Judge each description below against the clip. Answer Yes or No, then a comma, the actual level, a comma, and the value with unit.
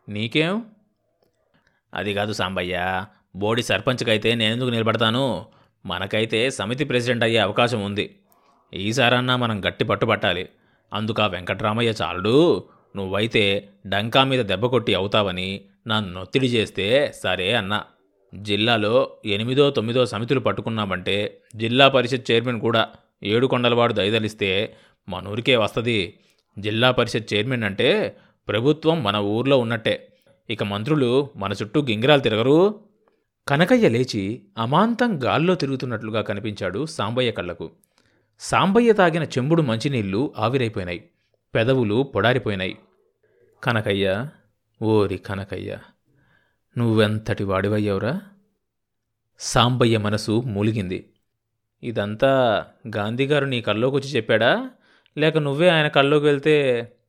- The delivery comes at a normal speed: Yes, average, 100 wpm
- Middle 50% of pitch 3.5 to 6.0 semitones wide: Yes, average, 4.5 semitones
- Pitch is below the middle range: Yes, low, 115 Hz